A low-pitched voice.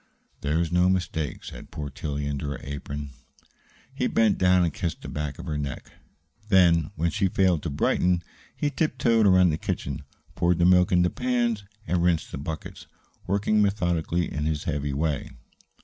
Yes: very low, 85 Hz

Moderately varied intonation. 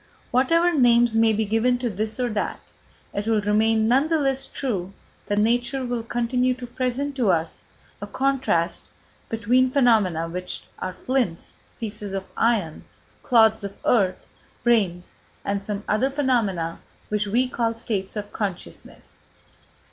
Yes: average, 3.8 semitones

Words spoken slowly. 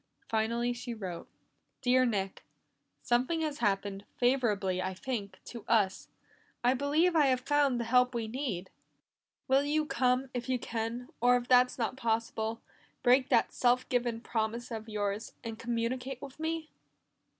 No: average, 150 wpm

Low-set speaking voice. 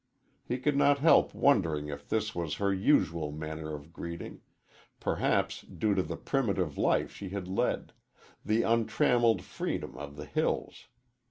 Yes: very low, 95 Hz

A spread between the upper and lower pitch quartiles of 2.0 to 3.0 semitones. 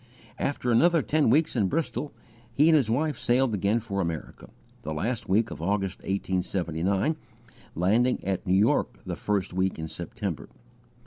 No: average, 5.3 semitones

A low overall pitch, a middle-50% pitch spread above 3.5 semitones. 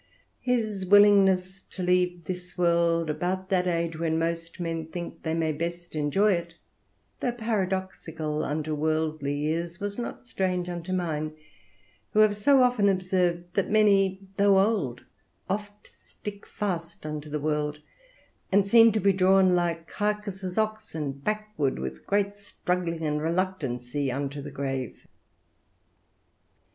No: medium, 180 Hz; average, 4.1 semitones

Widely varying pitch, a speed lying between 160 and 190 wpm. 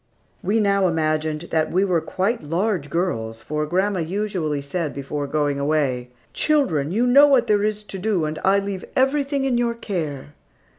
Yes: wide, 5.7 semitones; average, 170 wpm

